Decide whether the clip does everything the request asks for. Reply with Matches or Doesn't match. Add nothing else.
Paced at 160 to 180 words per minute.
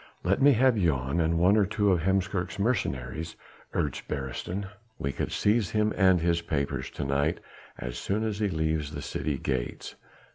Matches